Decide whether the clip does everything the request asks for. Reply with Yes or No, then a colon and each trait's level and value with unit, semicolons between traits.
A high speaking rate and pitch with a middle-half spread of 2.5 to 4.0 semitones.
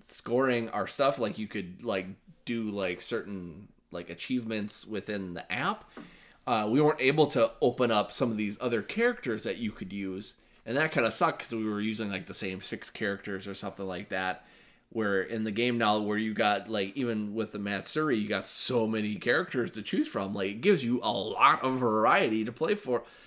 Yes: fast, 210 wpm; average, 3.3 semitones